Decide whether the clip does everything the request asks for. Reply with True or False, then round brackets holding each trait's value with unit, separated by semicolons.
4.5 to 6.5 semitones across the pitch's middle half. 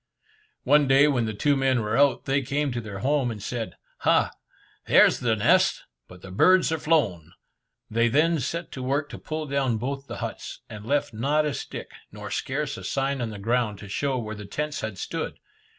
True (4.8 semitones)